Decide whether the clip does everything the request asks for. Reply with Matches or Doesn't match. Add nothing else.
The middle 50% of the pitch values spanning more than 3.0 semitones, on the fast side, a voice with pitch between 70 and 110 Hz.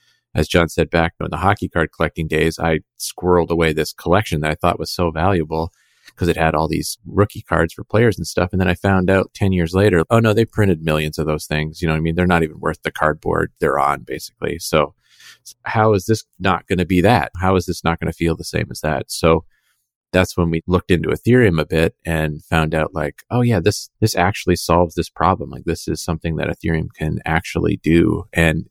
Doesn't match